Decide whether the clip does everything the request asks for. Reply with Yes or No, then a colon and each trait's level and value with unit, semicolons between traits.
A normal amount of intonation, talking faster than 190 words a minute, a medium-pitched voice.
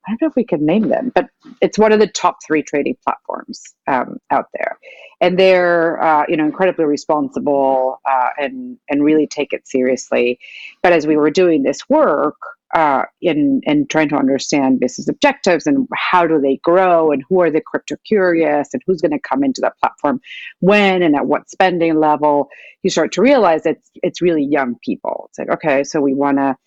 Yes: average, 4.8 semitones; fast, 205 wpm; medium, 165 Hz